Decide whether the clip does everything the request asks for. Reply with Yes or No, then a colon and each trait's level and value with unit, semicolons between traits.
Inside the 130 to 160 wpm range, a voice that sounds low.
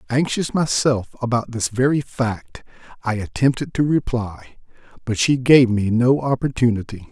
Yes: slow, 135 wpm; low, 125 Hz